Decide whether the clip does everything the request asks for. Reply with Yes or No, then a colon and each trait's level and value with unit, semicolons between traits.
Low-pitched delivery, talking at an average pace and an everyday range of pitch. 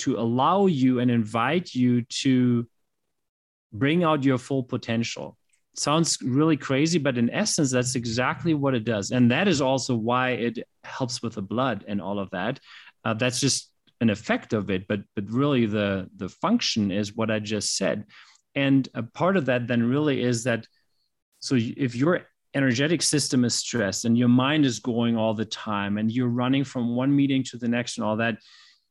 Yes: low, 125 Hz; average, 190 wpm; average, 3.0 semitones